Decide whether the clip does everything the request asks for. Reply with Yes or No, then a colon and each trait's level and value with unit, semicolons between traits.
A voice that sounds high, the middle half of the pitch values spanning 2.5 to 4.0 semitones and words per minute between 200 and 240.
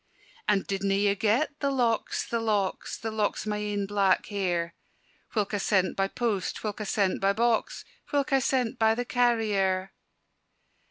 No: high, 210 Hz; average, 2.9 semitones; average, 170 wpm